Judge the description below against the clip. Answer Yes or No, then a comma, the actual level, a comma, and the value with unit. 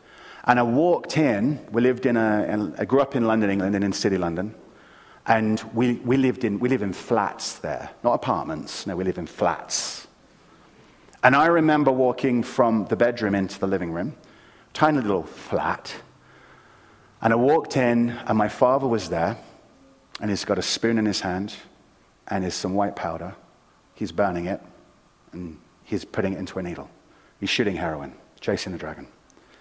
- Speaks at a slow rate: No, average, 180 wpm